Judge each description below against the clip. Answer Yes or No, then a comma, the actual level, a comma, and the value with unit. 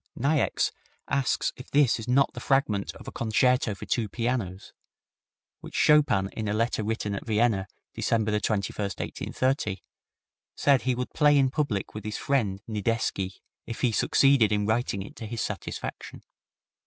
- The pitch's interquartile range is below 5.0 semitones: Yes, average, 3.9 semitones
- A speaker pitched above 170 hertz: No, low, 115 Hz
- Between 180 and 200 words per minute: No, average, 155 wpm